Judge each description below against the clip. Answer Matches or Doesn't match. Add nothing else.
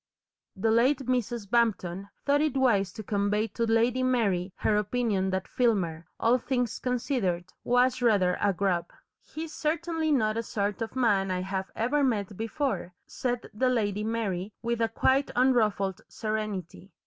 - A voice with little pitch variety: Doesn't match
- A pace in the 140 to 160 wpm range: Matches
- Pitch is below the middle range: Doesn't match